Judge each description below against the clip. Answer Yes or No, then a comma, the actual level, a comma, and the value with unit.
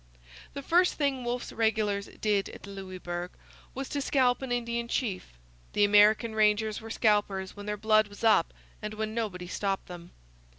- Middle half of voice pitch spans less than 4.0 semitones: Yes, average, 2.8 semitones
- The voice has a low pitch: No, high, 215 Hz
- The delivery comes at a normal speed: Yes, average, 165 wpm